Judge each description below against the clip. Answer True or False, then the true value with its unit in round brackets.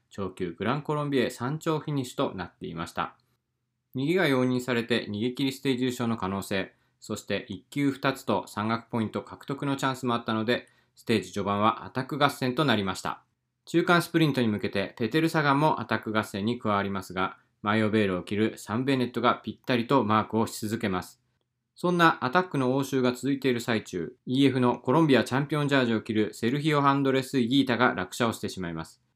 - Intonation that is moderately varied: True (4.1 semitones)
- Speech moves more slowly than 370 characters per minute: False (440 characters per minute)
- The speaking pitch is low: True (120 Hz)